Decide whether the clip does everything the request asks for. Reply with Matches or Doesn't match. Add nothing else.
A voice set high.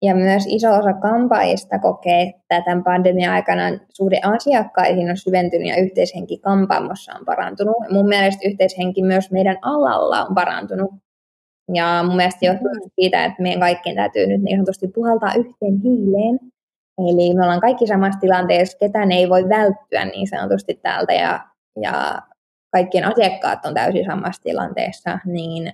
Matches